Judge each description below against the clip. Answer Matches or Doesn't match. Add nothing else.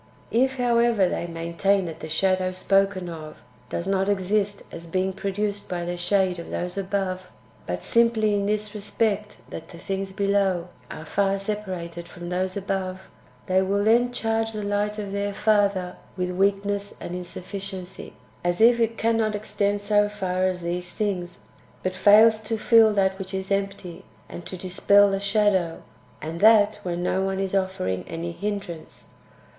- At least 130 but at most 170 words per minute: Matches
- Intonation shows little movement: Matches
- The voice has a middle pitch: Doesn't match